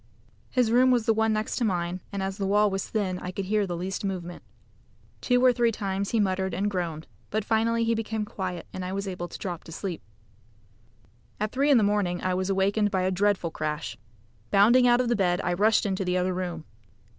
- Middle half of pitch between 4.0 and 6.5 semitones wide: No, average, 3.1 semitones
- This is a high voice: Yes, high, 195 Hz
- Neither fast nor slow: No, fast, 220 wpm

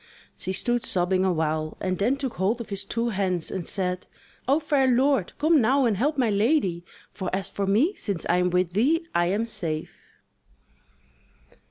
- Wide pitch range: Yes, wide, 5.9 semitones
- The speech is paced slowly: No, average, 180 wpm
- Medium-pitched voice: No, high, 200 Hz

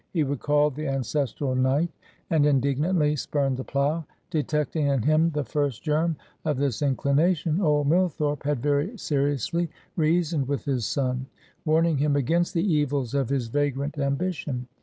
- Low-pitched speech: No, medium, 145 Hz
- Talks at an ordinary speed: Yes, average, 150 wpm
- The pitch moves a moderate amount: No, narrow, 2.3 semitones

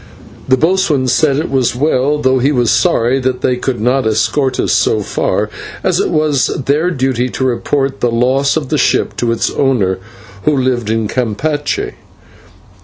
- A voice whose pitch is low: Yes, low, 130 Hz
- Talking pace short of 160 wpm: No, average, 175 wpm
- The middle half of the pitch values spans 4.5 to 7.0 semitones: No, average, 3.0 semitones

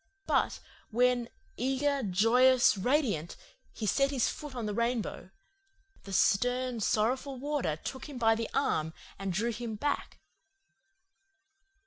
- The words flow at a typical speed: No, slow, 125 wpm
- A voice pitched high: Yes, high, 240 Hz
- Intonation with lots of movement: No, average, 3.7 semitones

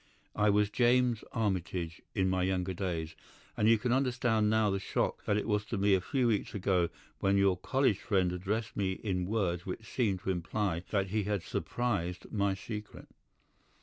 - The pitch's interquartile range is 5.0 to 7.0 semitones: No, average, 3.0 semitones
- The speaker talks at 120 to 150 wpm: No, average, 180 wpm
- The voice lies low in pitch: Yes, low, 100 Hz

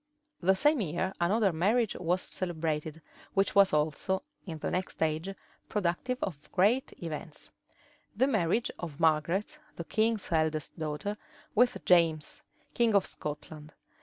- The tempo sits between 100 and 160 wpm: Yes, slow, 135 wpm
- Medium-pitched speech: Yes, medium, 175 Hz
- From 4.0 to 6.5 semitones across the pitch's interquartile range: Yes, average, 4.5 semitones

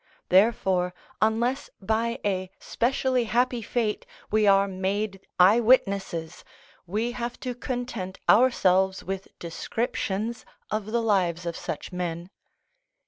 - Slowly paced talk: Yes, slow, 115 wpm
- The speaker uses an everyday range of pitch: Yes, average, 4.0 semitones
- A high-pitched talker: Yes, high, 210 Hz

